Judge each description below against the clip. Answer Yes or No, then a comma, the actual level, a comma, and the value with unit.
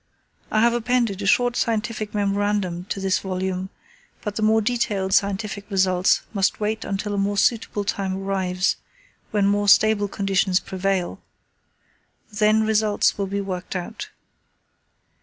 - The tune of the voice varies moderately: No, narrow, 1.9 semitones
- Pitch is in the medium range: No, high, 200 Hz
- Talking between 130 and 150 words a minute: Yes, average, 140 wpm